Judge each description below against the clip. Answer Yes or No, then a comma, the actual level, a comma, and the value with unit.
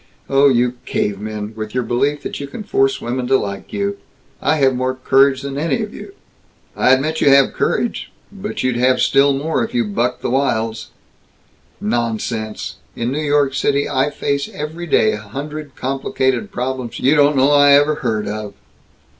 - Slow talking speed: No, average, 175 wpm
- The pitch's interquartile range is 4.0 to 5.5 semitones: No, average, 3.5 semitones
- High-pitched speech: No, low, 135 Hz